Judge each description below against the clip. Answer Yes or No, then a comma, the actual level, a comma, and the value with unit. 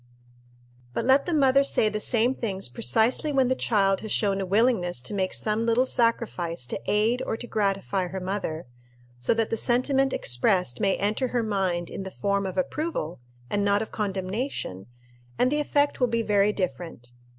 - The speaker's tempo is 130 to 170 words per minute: No, average, 185 wpm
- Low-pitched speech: No, high, 210 Hz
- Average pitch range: Yes, average, 4.4 semitones